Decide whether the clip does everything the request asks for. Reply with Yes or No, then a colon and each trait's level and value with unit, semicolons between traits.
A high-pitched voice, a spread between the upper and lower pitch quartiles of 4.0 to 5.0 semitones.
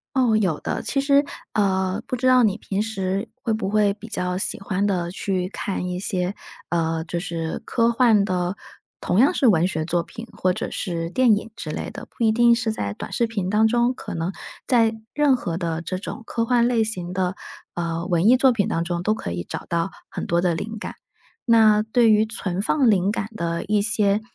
Yes: high, 200 Hz; average, 4.3 semitones